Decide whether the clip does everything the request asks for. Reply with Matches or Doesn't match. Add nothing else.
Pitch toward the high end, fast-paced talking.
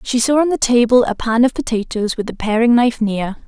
Matches